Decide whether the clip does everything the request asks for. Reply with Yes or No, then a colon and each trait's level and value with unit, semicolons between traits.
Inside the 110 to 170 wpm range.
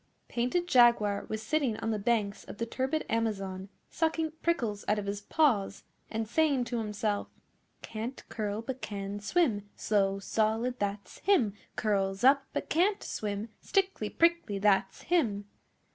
Yes: average, 145 wpm